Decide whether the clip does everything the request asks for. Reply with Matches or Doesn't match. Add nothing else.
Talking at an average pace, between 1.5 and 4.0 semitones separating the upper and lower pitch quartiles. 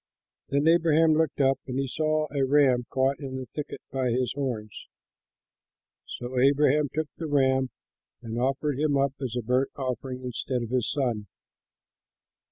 Matches